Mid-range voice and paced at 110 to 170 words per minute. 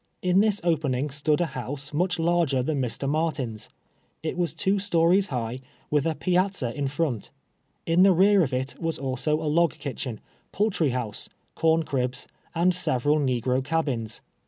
Yes: medium, 150 Hz; average, 160 wpm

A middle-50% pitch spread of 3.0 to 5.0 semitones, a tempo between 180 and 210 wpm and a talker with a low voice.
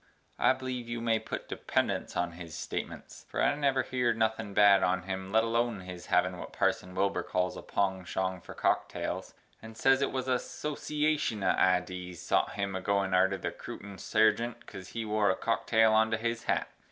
Yes: average, 3.9 semitones; average, 185 wpm; low, 105 Hz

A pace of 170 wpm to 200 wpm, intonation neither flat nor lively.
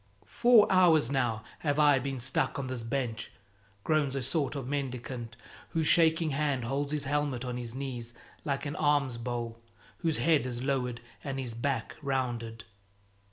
No: average, 160 wpm; average, 3.3 semitones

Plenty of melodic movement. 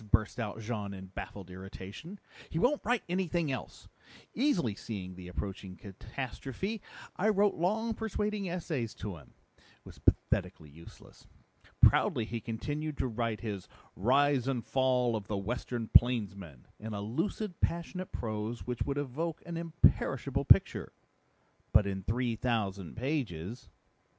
Yes: wide, 8.2 semitones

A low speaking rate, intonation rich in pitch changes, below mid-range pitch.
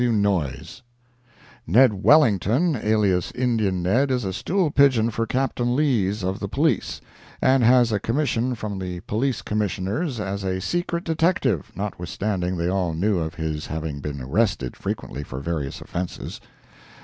No: average, 150 wpm; wide, 5.7 semitones; low, 105 Hz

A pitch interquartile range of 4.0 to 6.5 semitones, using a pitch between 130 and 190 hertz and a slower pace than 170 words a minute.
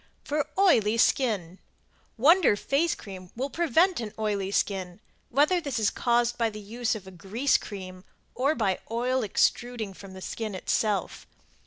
No: average, 5.2 semitones; high, 225 Hz; average, 155 wpm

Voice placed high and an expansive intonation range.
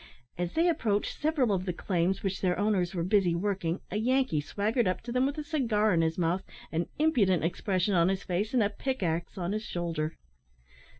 No: high, 195 Hz; average, 4.6 semitones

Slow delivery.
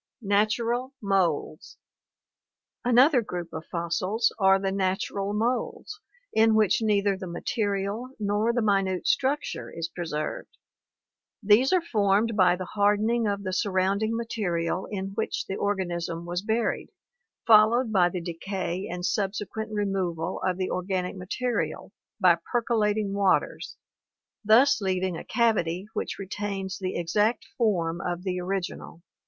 Yes: slow, 130 wpm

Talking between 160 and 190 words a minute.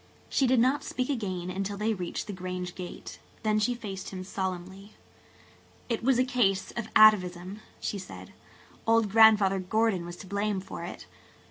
Yes: average, 165 wpm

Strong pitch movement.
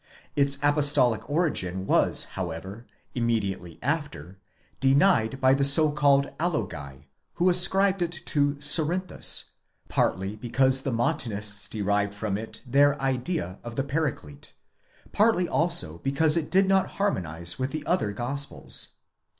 Yes: wide, 7.1 semitones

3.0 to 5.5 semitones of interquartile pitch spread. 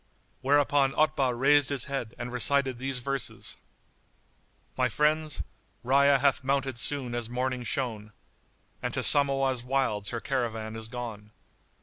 No: narrow, 2.6 semitones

